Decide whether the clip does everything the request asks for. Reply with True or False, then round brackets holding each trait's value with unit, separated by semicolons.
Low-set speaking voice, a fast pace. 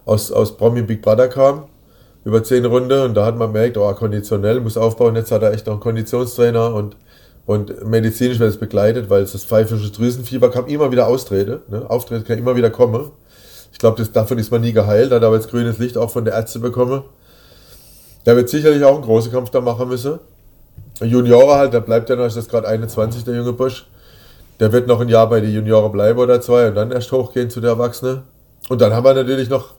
True (120 Hz; 220 wpm)